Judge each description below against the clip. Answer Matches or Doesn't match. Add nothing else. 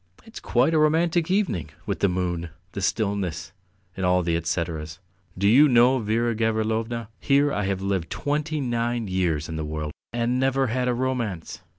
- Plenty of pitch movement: Matches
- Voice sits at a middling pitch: Doesn't match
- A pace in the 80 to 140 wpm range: Doesn't match